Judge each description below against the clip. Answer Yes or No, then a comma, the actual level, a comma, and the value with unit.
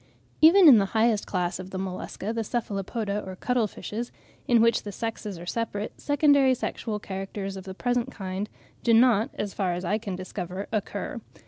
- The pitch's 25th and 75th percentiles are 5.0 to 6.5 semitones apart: No, average, 3.5 semitones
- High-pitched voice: Yes, high, 210 Hz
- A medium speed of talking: Yes, average, 185 wpm